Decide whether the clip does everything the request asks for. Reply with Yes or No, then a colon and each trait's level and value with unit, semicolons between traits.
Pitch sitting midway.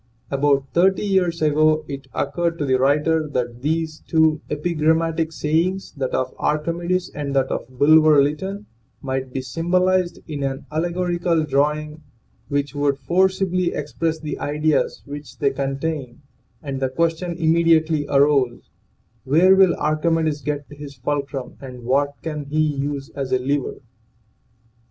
Yes: medium, 150 Hz